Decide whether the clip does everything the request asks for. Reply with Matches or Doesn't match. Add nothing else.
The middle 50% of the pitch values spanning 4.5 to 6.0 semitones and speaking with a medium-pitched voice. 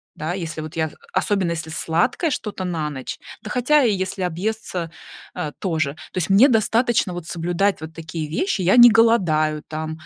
Matches